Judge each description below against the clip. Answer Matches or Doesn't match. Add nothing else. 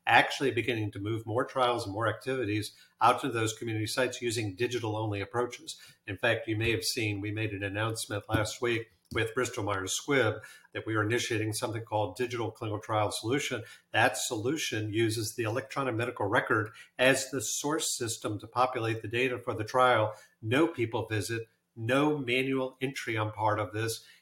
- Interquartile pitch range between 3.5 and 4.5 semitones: Doesn't match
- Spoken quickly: Doesn't match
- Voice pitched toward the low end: Matches